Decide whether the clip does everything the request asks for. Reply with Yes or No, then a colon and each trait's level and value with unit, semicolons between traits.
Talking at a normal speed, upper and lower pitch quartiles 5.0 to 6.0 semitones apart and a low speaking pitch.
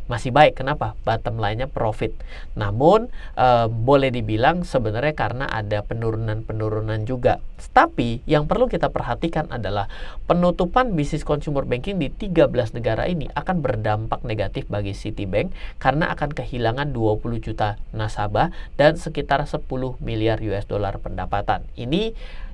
Yes: average, 130 wpm; wide, 5.4 semitones; low, 120 Hz